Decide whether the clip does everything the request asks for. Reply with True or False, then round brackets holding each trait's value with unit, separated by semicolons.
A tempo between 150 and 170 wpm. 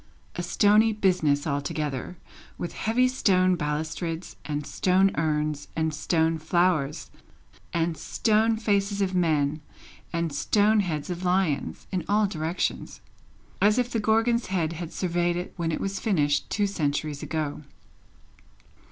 False (135 wpm)